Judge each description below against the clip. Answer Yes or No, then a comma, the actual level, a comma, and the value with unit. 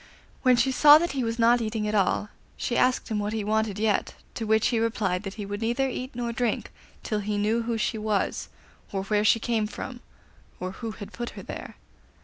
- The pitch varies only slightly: Yes, narrow, 2.3 semitones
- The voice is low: No, high, 220 Hz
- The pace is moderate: No, fast, 220 wpm